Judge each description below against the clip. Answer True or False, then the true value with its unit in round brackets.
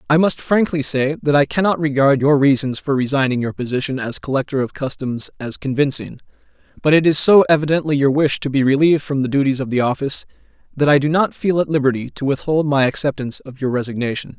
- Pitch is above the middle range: False (140 Hz)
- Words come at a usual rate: False (210 wpm)